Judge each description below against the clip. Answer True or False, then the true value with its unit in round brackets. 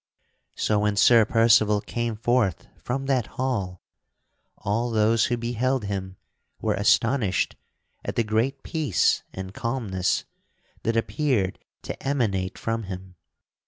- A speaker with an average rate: False (125 wpm)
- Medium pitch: False (115 Hz)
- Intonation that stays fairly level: False (3.4 semitones)